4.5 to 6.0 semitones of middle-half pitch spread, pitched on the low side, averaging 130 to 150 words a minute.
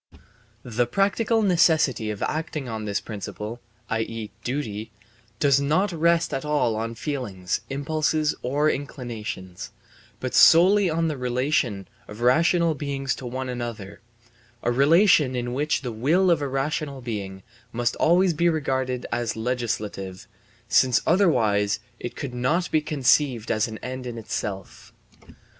Yes: average, 5.2 semitones; low, 130 Hz; average, 140 wpm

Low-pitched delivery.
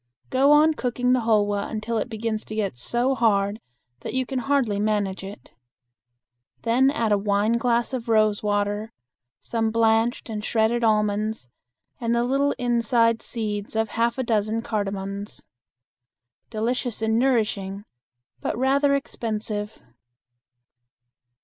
No: high, 225 Hz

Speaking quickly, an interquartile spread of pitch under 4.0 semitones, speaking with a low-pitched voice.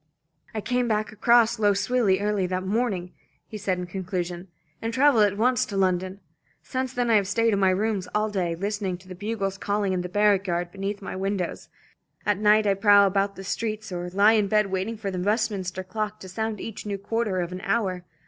No: fast, 215 wpm; narrow, 2.5 semitones; high, 200 Hz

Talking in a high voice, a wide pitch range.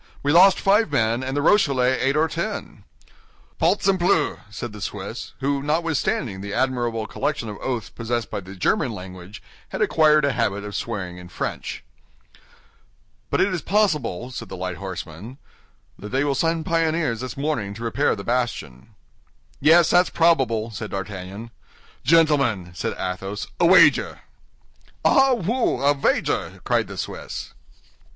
No: low, 125 Hz; wide, 7.4 semitones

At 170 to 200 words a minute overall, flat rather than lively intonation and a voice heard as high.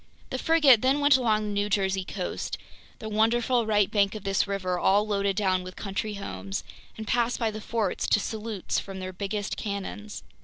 Yes: average, 180 wpm; narrow, 2.2 semitones; high, 210 Hz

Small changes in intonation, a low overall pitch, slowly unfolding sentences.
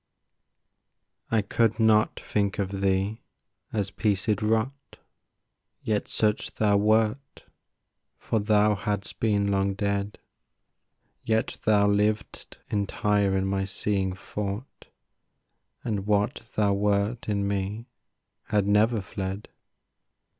Yes: narrow, 1.5 semitones; low, 105 Hz; slow, 105 wpm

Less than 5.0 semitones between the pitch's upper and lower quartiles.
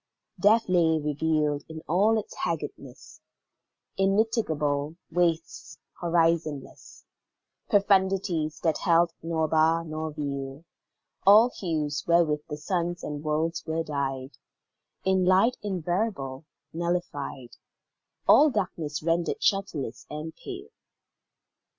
Yes: average, 3.7 semitones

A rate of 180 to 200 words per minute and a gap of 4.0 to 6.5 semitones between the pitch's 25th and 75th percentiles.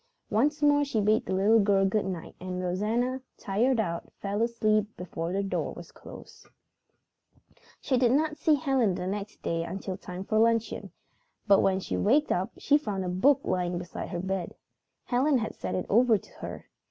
Yes: average, 185 wpm; average, 4.8 semitones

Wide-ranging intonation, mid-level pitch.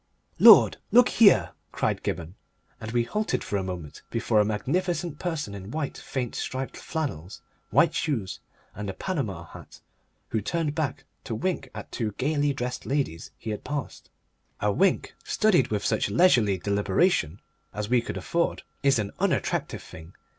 No: wide, 7.2 semitones; low, 120 Hz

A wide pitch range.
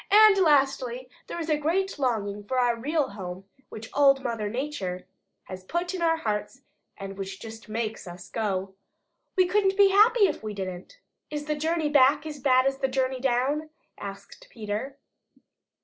Yes: wide, 6.6 semitones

